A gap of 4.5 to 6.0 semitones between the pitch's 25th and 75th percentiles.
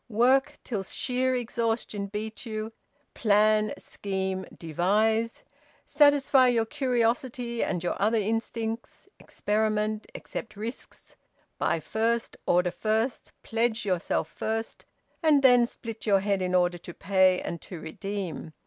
No: average, 3.3 semitones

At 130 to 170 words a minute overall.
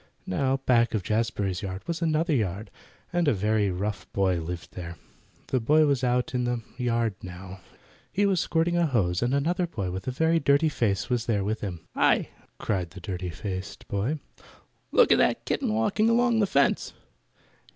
No: average, 180 wpm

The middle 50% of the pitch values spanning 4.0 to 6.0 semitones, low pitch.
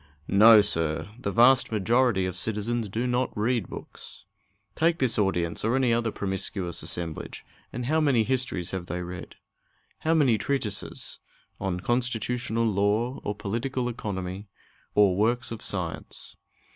Yes: average, 4.4 semitones; low, 110 Hz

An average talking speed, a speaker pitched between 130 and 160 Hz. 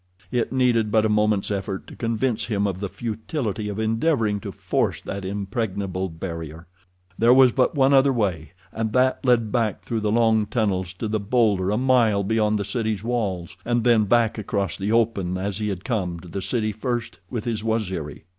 No: average, 195 wpm; low, 110 Hz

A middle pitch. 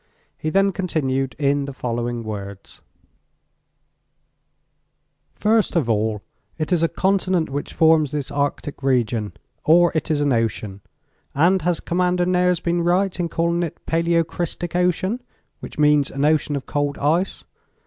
Yes: medium, 155 Hz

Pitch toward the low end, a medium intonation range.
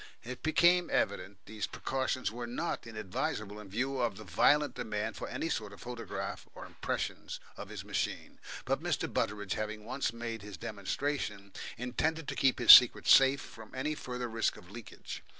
Yes: low, 115 Hz; average, 4.0 semitones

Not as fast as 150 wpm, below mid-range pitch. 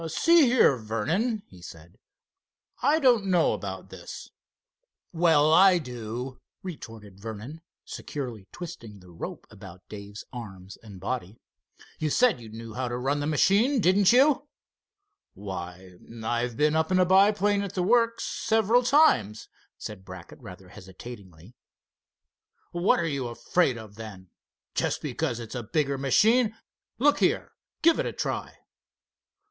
Yes: average, 140 wpm; low, 130 Hz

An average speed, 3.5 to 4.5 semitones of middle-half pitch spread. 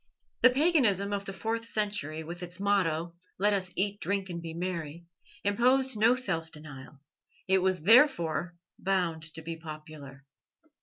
Yes: average, 150 wpm; average, 4.1 semitones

